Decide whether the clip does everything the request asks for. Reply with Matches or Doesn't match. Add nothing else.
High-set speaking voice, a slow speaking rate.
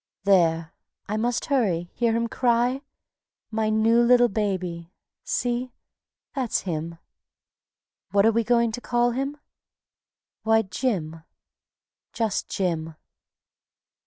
Matches